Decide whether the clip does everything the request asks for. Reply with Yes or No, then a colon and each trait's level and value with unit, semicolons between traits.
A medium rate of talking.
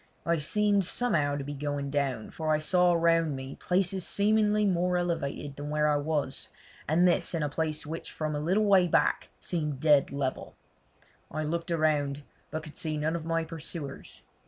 Yes: average, 180 wpm